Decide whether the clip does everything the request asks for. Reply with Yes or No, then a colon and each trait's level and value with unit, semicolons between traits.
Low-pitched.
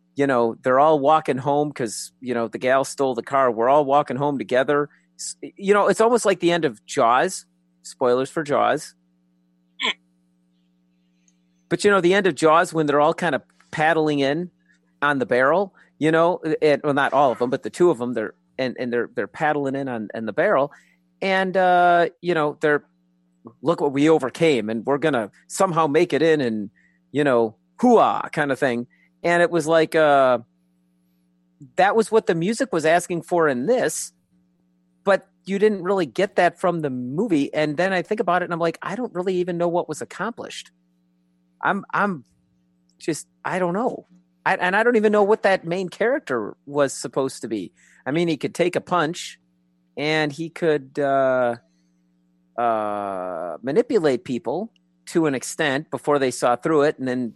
No: medium, 145 Hz